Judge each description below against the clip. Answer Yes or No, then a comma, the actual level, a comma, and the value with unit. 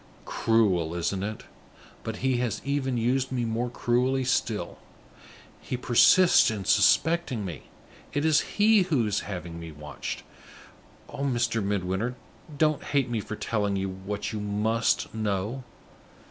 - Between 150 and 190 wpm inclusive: No, average, 140 wpm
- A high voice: No, low, 115 Hz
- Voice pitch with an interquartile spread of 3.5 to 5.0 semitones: Yes, average, 4.5 semitones